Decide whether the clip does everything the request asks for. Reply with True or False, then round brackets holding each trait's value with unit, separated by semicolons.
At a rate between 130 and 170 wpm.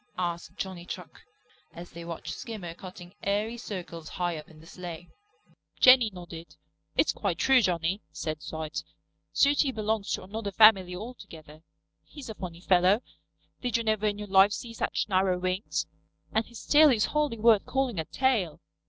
True (165 wpm)